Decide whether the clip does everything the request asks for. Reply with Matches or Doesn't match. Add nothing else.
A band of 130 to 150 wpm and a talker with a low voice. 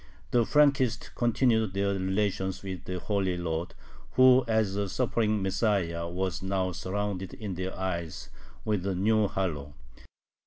Matches